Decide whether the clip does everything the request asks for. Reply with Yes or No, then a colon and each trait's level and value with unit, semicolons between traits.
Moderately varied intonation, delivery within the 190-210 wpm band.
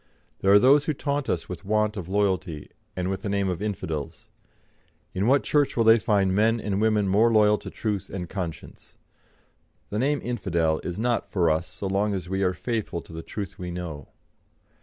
Yes: average, 3.4 semitones; average, 200 wpm